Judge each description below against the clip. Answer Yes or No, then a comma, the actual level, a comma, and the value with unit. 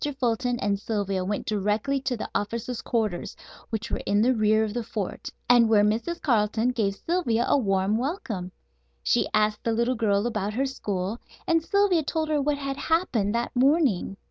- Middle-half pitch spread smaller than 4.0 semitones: No, average, 4.3 semitones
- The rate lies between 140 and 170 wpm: No, average, 180 wpm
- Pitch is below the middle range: No, high, 230 Hz